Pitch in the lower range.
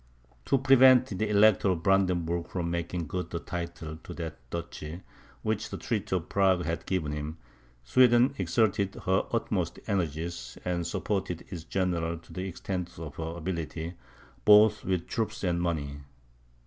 Yes: very low, 90 Hz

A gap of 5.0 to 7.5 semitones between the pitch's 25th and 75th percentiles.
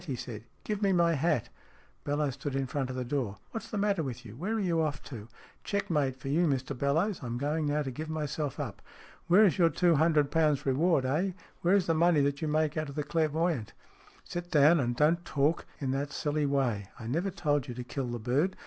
No: average, 4.0 semitones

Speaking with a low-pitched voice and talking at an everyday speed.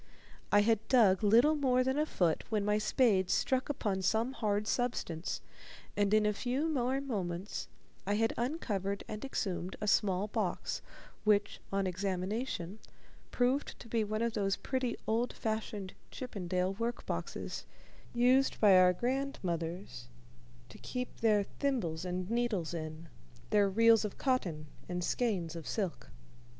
No: high, 210 Hz; average, 145 wpm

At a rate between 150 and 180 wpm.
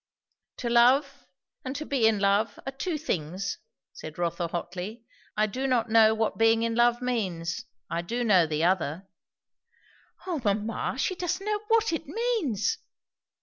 Yes: average, 155 wpm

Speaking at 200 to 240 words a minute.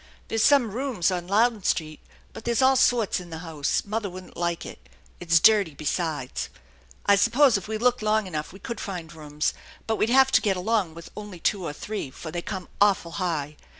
Yes: fast, 205 wpm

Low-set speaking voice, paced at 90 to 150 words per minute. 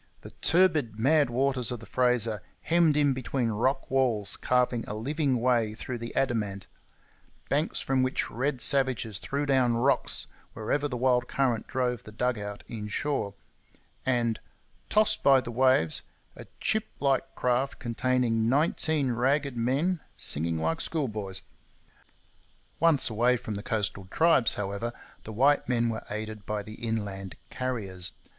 Yes: low, 125 Hz; average, 145 wpm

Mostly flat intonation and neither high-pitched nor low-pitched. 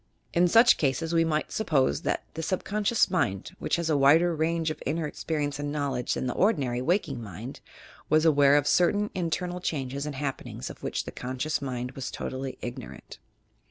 No: average, 3.9 semitones; medium, 150 Hz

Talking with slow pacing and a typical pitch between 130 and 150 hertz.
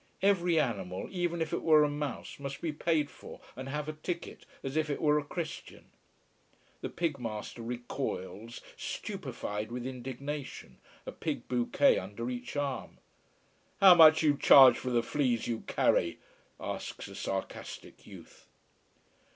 No: average, 150 wpm; medium, 140 Hz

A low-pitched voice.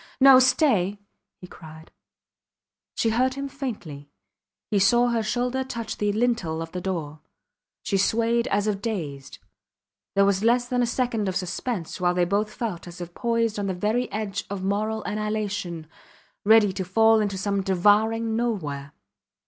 No: high, 210 Hz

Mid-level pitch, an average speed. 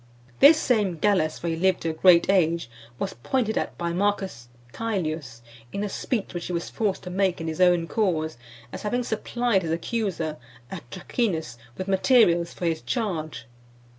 Yes: medium, 180 Hz; average, 170 wpm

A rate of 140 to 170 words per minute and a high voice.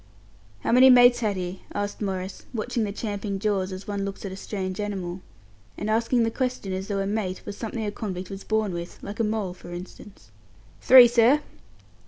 No: average, 200 wpm; high, 205 Hz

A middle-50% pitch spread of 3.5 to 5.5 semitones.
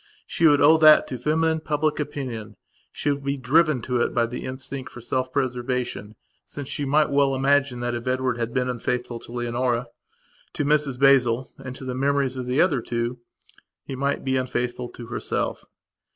No: narrow, 2.6 semitones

